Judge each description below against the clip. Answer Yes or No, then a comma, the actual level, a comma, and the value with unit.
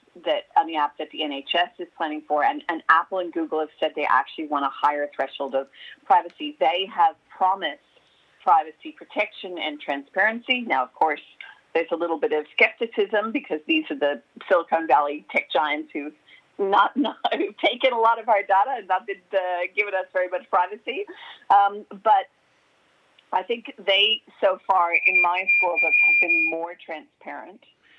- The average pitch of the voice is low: No, medium, 185 Hz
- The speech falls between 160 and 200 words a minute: Yes, average, 180 wpm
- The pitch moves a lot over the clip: Yes, wide, 6.7 semitones